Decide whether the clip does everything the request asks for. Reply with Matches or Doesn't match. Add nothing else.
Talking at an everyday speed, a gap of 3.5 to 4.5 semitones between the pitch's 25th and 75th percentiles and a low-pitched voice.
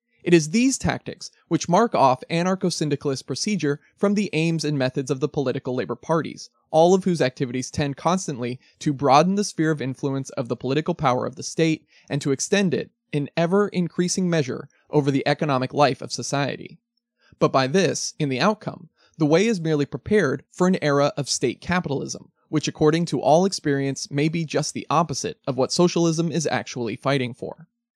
Doesn't match